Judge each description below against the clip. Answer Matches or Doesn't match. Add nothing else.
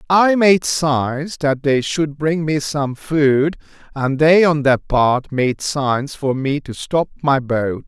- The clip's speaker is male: Matches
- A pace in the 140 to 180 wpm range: Matches